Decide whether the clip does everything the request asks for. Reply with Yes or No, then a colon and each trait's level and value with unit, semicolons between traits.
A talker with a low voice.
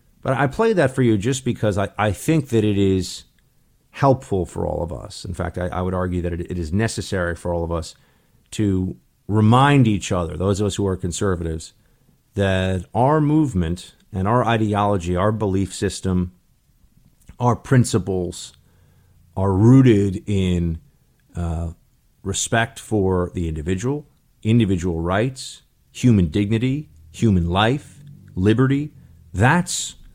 Yes: low, 100 Hz